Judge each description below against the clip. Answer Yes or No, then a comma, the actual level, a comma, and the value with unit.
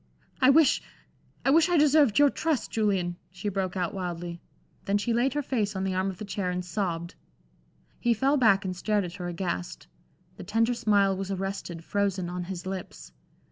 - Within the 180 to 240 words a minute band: Yes, average, 190 wpm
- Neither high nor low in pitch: No, high, 195 Hz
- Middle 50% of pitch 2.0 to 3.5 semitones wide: No, average, 4.1 semitones